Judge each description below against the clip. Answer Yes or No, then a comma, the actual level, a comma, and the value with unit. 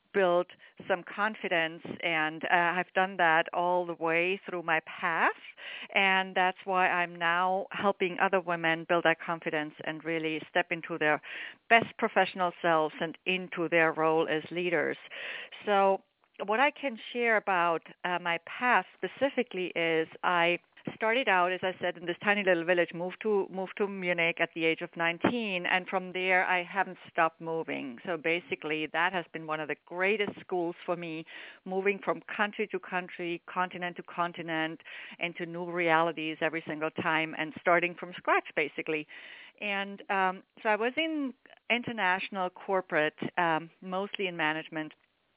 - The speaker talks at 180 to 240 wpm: No, average, 160 wpm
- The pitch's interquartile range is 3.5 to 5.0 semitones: No, narrow, 2.5 semitones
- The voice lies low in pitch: No, medium, 180 Hz